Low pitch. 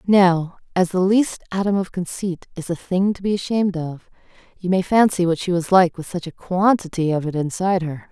No: medium, 180 Hz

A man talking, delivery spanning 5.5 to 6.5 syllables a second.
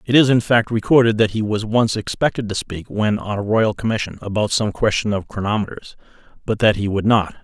Yes: male; 5.6 syllables/s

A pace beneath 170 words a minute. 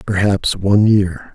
Yes: slow, 135 wpm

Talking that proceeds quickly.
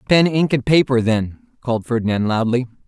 No: average, 165 wpm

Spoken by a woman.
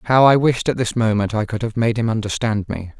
No: male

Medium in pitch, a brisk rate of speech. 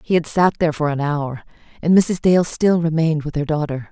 Yes: medium, 160 Hz; fast, 230 wpm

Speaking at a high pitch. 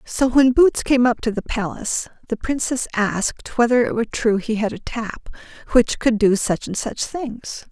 Yes: high, 235 Hz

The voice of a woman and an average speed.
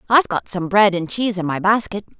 No: female; fast, 245 wpm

